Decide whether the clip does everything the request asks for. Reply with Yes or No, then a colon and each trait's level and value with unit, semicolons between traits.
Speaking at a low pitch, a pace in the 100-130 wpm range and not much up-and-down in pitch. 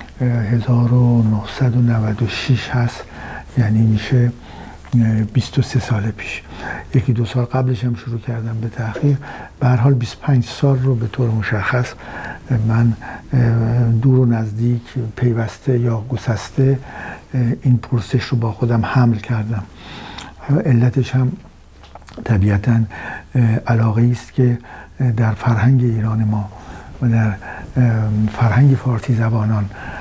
Yes: low, 120 Hz; average, 110 wpm; narrow, 2.3 semitones